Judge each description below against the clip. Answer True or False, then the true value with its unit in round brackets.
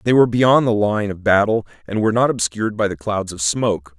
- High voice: False (105 Hz)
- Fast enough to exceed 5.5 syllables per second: True (6.0 syllables/s)